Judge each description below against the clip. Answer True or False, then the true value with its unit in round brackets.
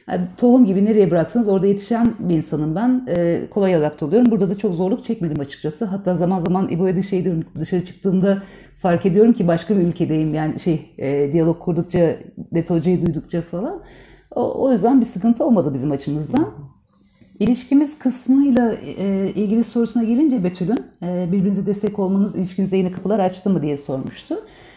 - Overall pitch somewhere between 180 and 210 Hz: True (190 Hz)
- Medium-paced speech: False (160 wpm)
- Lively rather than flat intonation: False (4.8 semitones)